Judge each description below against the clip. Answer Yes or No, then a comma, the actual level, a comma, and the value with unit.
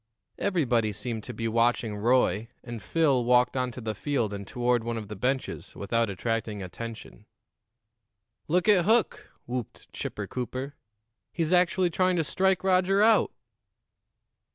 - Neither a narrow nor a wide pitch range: No, wide, 7.0 semitones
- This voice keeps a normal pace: Yes, average, 145 wpm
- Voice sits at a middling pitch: No, low, 125 Hz